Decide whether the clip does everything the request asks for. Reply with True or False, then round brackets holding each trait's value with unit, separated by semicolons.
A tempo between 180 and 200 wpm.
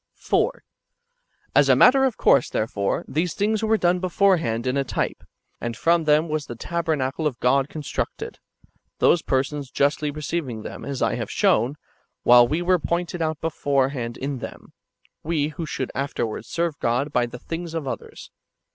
False (170 wpm)